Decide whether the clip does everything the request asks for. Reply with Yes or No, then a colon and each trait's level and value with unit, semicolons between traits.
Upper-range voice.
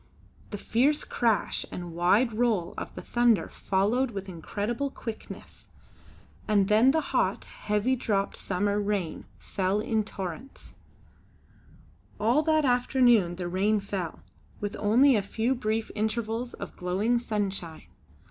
Yes: high, 215 Hz